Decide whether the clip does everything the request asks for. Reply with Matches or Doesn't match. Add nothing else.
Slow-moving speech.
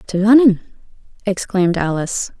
Matches